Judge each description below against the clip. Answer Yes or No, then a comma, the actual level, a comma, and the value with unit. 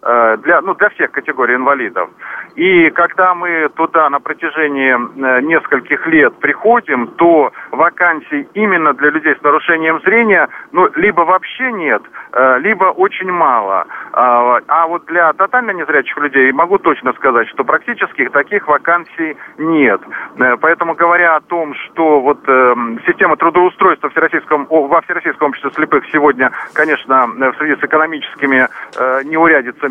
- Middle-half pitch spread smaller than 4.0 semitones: Yes, average, 3.4 semitones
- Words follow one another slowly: No, average, 130 wpm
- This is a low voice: No, medium, 155 Hz